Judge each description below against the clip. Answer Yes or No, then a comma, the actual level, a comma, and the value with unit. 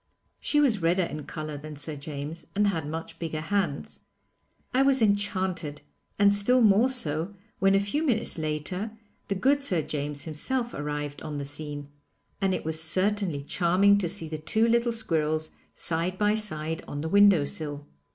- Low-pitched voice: No, medium, 170 Hz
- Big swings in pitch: No, average, 5.0 semitones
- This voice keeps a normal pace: Yes, average, 170 wpm